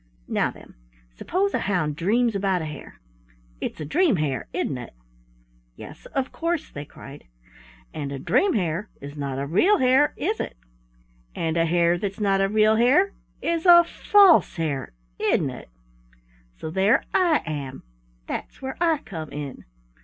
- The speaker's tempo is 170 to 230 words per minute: No, average, 160 wpm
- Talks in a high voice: Yes, high, 195 Hz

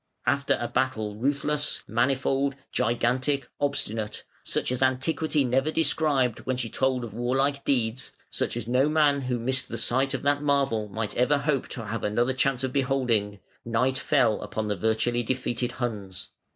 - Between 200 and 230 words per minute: No, average, 165 wpm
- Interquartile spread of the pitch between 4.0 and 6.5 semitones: No, average, 3.2 semitones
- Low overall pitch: Yes, low, 130 Hz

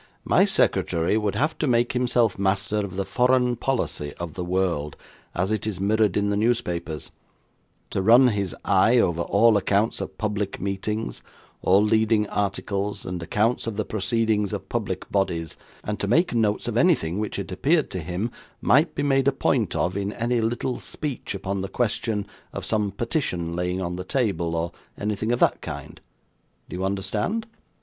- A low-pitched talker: Yes, low, 105 Hz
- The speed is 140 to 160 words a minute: No, average, 175 wpm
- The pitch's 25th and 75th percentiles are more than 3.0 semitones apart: Yes, average, 3.7 semitones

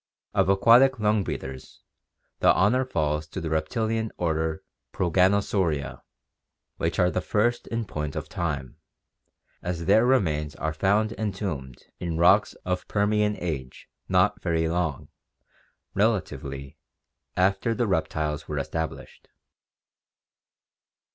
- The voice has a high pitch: No, very low, 90 Hz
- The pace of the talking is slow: Yes, slow, 115 wpm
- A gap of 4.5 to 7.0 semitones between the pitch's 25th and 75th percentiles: Yes, average, 5.1 semitones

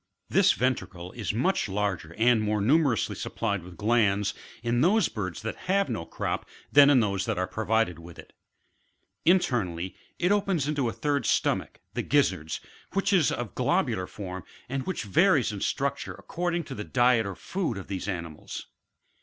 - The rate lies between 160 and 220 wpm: Yes, average, 170 wpm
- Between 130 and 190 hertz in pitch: No, low, 115 Hz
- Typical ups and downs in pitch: No, wide, 6.9 semitones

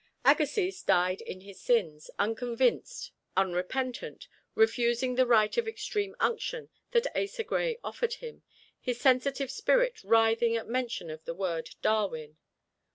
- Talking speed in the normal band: No, slow, 130 wpm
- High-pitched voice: Yes, high, 245 Hz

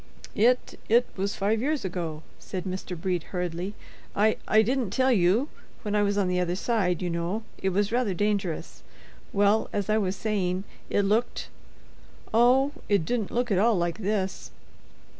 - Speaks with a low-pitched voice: No, high, 205 Hz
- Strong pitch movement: No, average, 3.4 semitones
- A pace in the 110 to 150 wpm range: Yes, average, 140 wpm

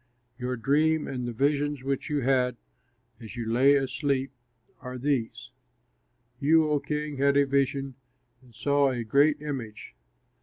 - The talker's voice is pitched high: No, low, 135 Hz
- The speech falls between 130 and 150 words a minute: Yes, average, 145 wpm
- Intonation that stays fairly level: Yes, narrow, 2.3 semitones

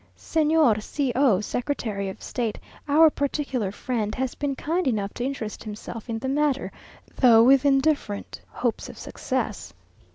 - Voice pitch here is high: Yes, very high, 255 Hz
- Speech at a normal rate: Yes, average, 150 wpm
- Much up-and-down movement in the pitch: No, average, 4.6 semitones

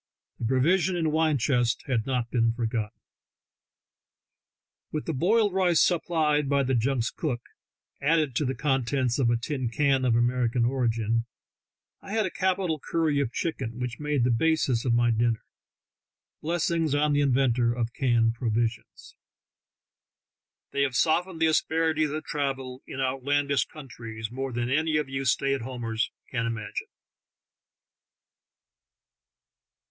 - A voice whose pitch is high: No, low, 135 Hz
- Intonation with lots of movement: No, average, 4.4 semitones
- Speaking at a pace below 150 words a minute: Yes, average, 140 wpm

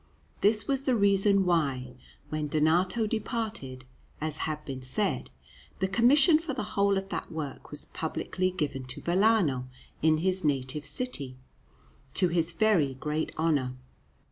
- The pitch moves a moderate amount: No, wide, 6.2 semitones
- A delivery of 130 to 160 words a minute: Yes, average, 145 wpm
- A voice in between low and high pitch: Yes, medium, 170 Hz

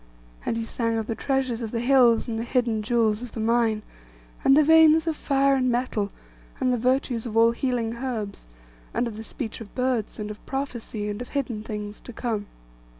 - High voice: Yes, high, 235 Hz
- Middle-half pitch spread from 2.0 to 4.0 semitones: Yes, average, 2.8 semitones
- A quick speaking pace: Yes, fast, 210 wpm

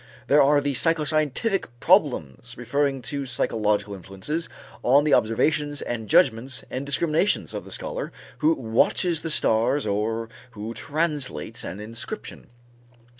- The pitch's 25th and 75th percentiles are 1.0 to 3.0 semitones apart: No, average, 5.3 semitones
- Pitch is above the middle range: No, low, 135 Hz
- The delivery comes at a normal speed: No, slow, 125 wpm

